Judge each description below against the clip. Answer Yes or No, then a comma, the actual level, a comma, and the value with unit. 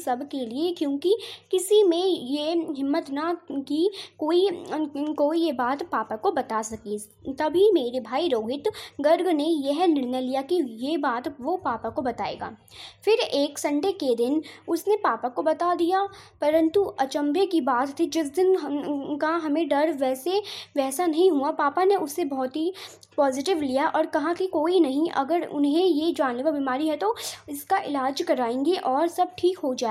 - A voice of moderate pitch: No, very high, 315 Hz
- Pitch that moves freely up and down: No, average, 4.2 semitones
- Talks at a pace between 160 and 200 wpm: Yes, average, 170 wpm